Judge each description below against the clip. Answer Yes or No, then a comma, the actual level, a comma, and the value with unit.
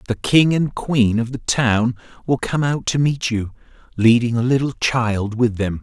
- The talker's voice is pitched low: Yes, low, 120 Hz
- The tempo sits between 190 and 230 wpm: Yes, average, 195 wpm